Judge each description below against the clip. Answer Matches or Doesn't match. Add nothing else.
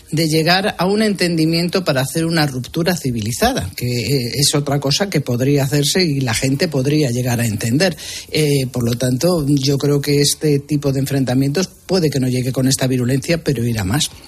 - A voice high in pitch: Doesn't match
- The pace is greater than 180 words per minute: Matches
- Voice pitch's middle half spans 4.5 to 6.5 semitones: Doesn't match